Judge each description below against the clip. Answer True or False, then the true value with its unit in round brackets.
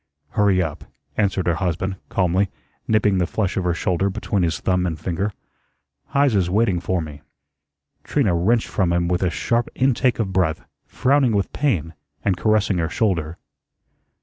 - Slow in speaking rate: False (160 wpm)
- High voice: False (95 Hz)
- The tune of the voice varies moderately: True (3.6 semitones)